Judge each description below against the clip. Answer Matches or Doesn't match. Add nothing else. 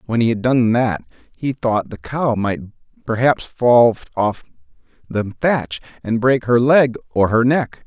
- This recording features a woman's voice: Doesn't match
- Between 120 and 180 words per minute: Matches